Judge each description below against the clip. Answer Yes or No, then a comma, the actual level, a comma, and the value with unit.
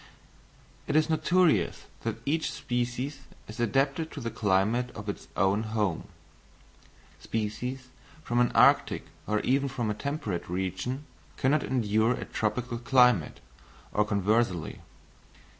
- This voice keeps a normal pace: No, slow, 125 wpm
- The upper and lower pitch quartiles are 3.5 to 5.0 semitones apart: Yes, average, 4.1 semitones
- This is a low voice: Yes, low, 120 Hz